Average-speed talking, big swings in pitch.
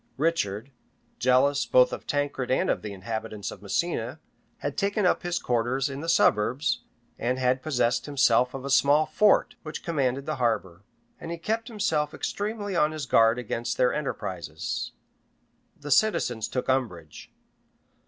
No: average, 155 wpm; average, 4.6 semitones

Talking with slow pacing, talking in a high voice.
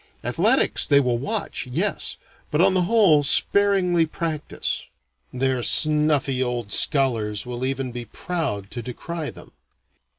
No: slow, 130 wpm; medium, 140 Hz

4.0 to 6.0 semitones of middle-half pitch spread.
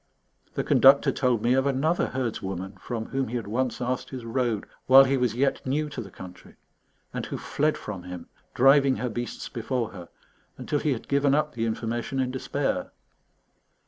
No: average, 3.1 semitones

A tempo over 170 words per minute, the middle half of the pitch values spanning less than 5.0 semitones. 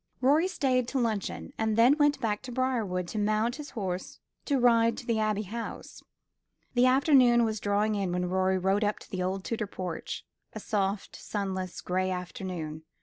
Yes: average, 180 wpm; average, 4.4 semitones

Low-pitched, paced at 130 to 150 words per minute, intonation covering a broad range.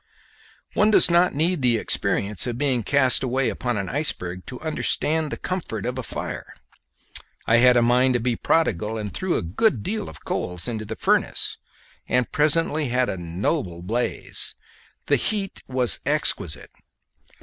No: low, 125 Hz; average, 160 wpm; wide, 5.8 semitones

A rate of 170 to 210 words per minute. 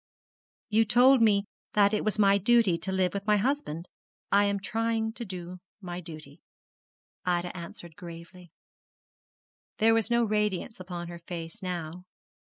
No: average, 155 wpm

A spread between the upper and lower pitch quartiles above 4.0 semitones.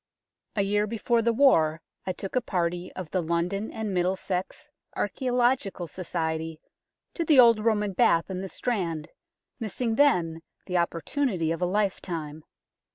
Yes: average, 5.2 semitones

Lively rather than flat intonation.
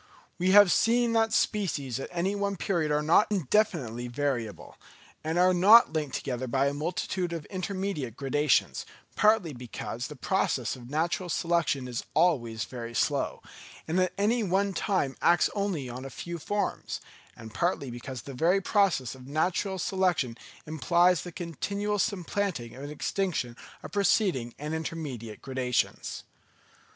Yes: wide, 6.5 semitones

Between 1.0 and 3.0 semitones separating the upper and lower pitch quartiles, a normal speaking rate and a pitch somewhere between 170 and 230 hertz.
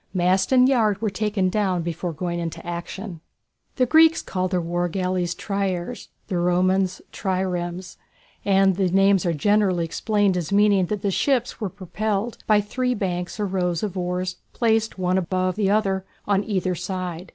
Yes: narrow, 2.5 semitones; average, 165 wpm; high, 190 Hz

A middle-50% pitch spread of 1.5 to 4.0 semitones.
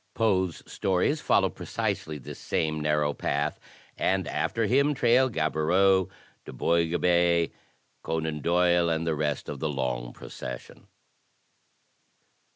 Yes: average, 3.7 semitones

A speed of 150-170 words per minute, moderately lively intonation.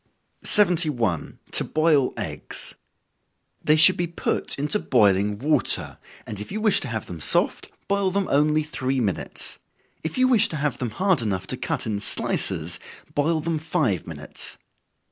No: average, 160 wpm; wide, 7.4 semitones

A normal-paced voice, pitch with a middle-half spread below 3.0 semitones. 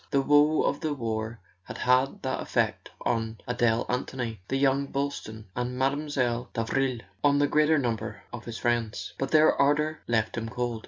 No: average, 170 wpm; average, 3.5 semitones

